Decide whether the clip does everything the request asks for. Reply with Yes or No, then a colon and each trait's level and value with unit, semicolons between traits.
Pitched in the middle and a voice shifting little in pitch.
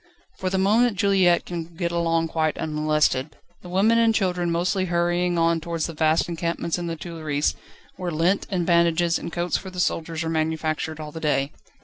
Yes: medium, 170 Hz; narrow, 1.9 semitones